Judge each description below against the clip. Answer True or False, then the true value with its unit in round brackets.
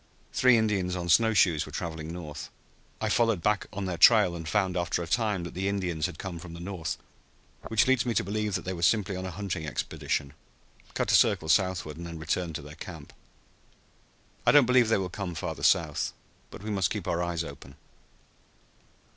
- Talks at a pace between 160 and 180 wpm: False (205 wpm)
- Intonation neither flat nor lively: True (3.8 semitones)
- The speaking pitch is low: True (90 Hz)